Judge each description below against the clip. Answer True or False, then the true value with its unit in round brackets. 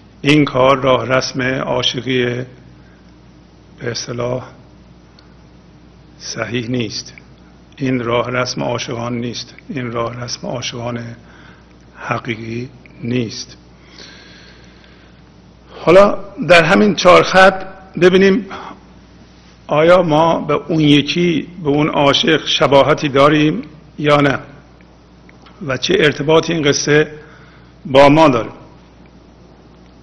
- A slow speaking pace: True (90 wpm)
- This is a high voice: False (125 Hz)